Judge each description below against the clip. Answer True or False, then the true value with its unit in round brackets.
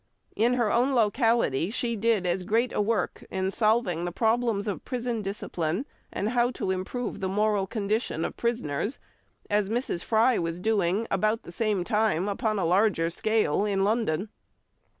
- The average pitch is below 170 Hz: False (210 Hz)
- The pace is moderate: True (165 wpm)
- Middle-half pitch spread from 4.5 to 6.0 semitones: False (3.5 semitones)